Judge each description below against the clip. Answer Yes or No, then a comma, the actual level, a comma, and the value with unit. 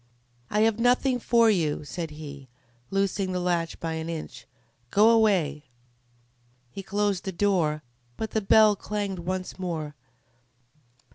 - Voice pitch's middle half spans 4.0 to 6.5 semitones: Yes, average, 4.5 semitones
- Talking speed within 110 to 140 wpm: Yes, slow, 135 wpm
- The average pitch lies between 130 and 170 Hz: No, medium, 185 Hz